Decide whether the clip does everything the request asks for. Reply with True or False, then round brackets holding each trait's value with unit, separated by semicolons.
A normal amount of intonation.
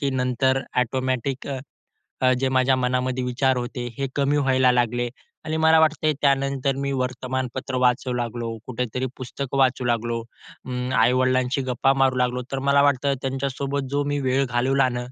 False (1.5 semitones)